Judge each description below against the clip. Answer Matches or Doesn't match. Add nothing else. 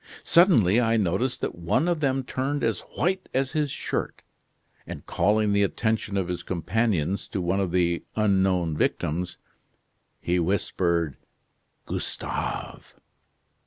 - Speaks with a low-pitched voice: Matches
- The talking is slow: Matches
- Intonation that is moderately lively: Doesn't match